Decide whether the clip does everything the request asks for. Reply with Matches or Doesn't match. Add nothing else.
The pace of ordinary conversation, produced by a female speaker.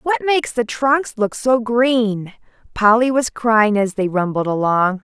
Matches